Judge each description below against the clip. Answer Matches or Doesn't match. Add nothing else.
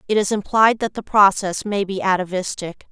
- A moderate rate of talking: Matches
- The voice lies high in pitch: Matches